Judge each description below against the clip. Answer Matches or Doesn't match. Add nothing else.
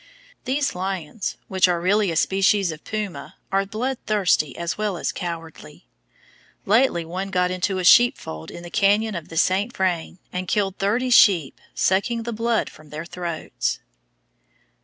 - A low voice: Doesn't match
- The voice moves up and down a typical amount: Matches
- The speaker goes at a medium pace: Matches